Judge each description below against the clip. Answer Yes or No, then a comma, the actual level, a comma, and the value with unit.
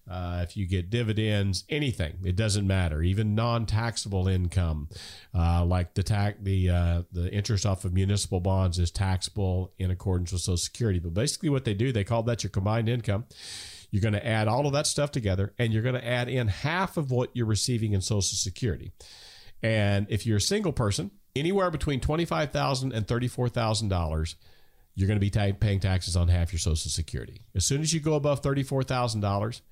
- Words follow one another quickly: No, average, 190 wpm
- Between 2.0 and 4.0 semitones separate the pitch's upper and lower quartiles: No, average, 4.6 semitones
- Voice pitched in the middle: No, low, 105 Hz